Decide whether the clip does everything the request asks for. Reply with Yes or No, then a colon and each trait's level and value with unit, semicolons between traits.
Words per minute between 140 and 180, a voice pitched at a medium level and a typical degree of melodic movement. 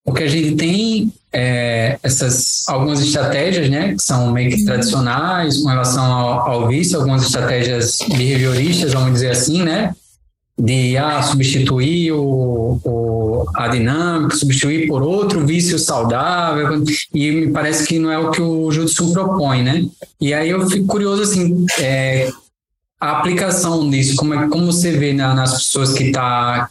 Yes: average, 155 wpm; medium, 145 Hz; average, 4.2 semitones